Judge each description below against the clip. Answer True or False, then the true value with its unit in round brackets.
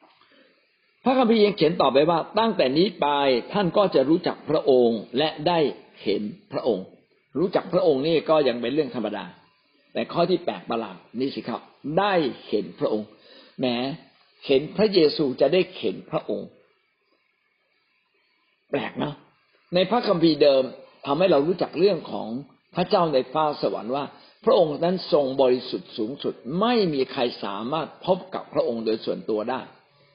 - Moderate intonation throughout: False (6.1 semitones)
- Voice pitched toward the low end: False (155 Hz)